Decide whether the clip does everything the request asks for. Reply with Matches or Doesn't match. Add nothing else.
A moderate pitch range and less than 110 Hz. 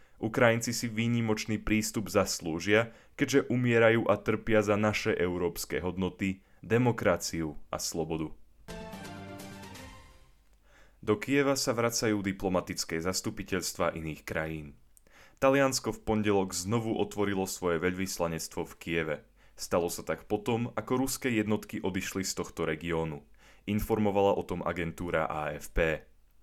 Matches